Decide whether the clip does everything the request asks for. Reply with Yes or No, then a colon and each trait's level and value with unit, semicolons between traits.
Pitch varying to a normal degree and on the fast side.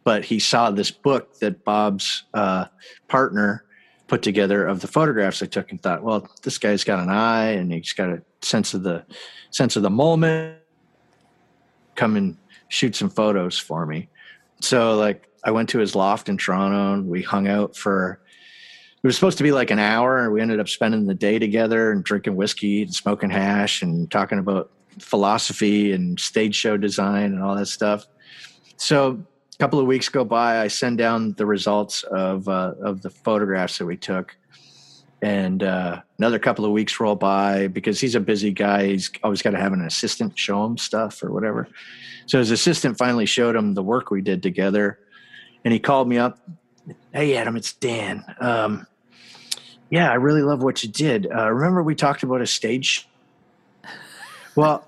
No: average, 4.0 semitones; average, 185 wpm